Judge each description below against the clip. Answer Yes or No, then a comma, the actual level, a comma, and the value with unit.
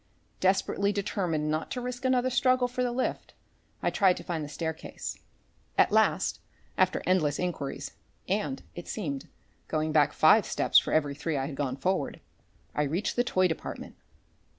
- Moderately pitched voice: Yes, medium, 175 Hz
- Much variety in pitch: Yes, wide, 6.0 semitones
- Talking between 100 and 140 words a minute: No, average, 165 wpm